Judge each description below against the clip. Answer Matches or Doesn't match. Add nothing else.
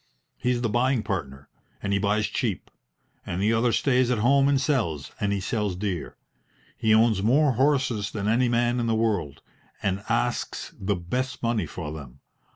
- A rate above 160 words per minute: Matches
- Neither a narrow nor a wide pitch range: Matches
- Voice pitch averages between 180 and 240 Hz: Doesn't match